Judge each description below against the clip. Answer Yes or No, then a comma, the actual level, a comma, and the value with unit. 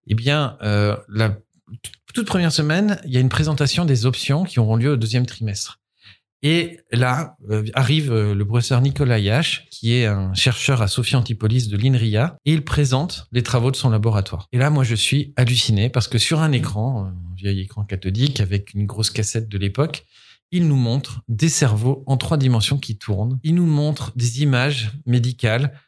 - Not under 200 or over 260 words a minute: No, average, 190 wpm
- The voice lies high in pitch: No, low, 125 Hz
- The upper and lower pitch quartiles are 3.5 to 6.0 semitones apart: Yes, average, 4.6 semitones